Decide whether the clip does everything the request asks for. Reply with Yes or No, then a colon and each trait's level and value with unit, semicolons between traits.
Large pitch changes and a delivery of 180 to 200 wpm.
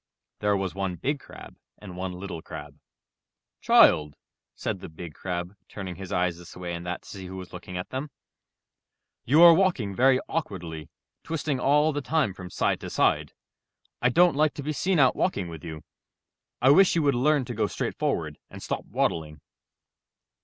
Yes: wide, 8.4 semitones; average, 185 wpm